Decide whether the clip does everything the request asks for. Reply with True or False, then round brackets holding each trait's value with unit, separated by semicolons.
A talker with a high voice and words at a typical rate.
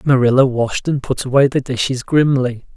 False (130 Hz; 175 wpm)